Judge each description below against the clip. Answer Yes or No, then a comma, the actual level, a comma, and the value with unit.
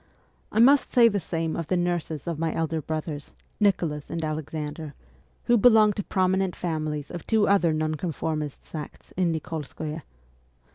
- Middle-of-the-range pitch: Yes, medium, 165 Hz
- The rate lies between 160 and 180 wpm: No, average, 150 wpm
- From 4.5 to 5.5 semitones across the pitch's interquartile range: No, average, 3.3 semitones